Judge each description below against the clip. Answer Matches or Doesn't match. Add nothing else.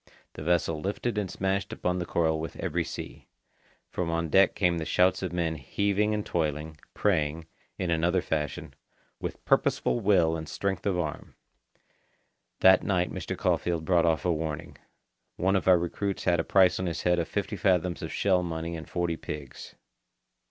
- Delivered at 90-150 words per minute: Doesn't match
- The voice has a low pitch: Matches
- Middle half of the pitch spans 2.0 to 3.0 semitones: Matches